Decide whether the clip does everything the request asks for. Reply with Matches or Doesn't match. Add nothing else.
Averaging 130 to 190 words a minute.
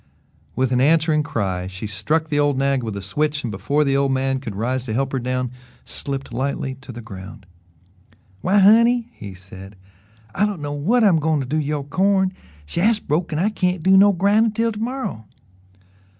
Doesn't match